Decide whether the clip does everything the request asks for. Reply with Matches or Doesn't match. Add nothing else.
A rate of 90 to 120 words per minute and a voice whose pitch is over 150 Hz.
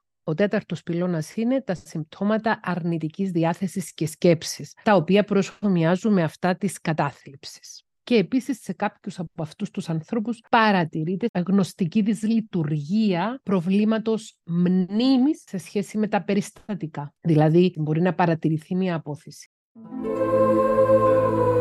Matches